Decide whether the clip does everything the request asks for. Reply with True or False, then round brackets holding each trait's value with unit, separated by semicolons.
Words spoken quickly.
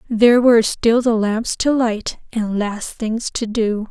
False (185 wpm)